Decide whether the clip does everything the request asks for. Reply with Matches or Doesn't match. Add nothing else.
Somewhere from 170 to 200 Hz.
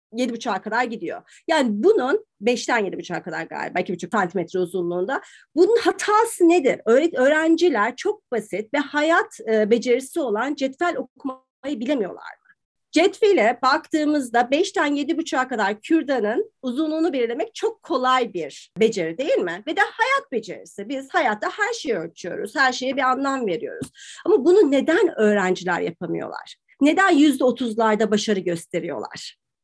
Doesn't match